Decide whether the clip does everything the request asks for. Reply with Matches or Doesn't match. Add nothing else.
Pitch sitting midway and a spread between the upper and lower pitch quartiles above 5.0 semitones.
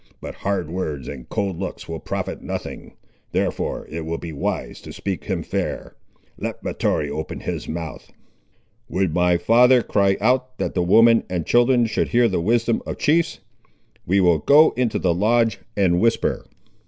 Doesn't match